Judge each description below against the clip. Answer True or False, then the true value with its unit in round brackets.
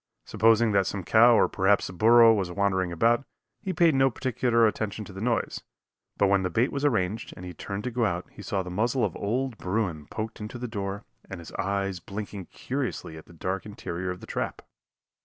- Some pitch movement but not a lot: True (3.7 semitones)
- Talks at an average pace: False (215 wpm)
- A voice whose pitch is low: True (105 Hz)